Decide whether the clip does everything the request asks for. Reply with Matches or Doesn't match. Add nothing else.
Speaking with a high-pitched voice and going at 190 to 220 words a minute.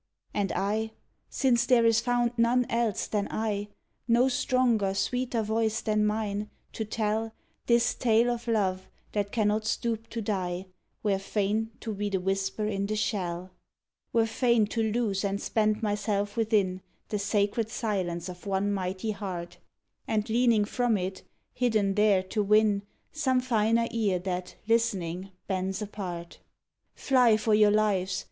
Doesn't match